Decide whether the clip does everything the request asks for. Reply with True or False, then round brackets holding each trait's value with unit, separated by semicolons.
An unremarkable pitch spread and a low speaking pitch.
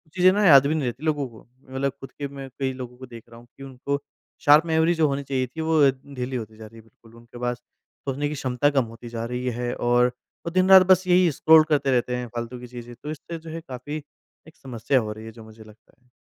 True (3.7 semitones; 130 Hz)